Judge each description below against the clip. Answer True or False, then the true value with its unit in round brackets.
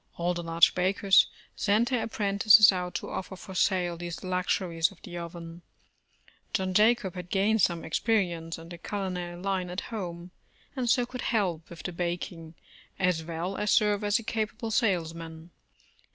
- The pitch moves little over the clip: False (3.2 semitones)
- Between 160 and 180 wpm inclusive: True (170 wpm)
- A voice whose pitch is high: False (180 Hz)